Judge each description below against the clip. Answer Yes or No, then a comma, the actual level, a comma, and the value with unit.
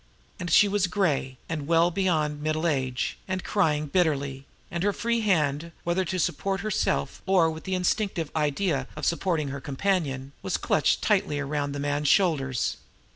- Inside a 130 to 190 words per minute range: Yes, average, 165 wpm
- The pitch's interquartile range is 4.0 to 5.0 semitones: Yes, average, 4.6 semitones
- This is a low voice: No, medium, 160 Hz